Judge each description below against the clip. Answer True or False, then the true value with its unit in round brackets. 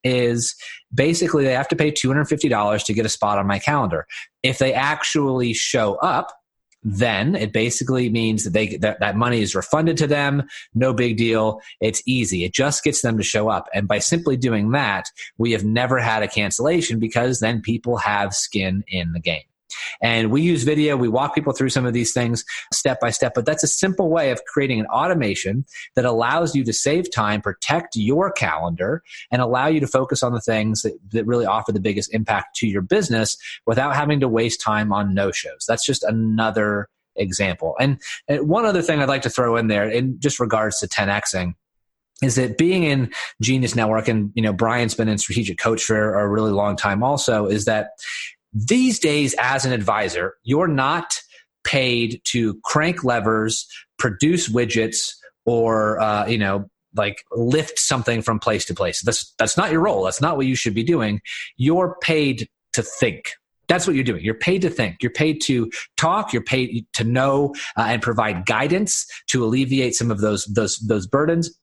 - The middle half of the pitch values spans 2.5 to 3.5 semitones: False (4.0 semitones)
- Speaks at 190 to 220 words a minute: True (195 wpm)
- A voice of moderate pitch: False (120 Hz)